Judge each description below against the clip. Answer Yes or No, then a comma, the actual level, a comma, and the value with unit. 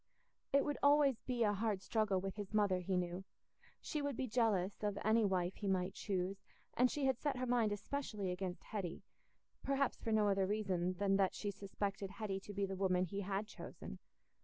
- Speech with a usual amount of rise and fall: Yes, average, 3.0 semitones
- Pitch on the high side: Yes, high, 200 Hz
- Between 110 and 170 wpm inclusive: No, average, 195 wpm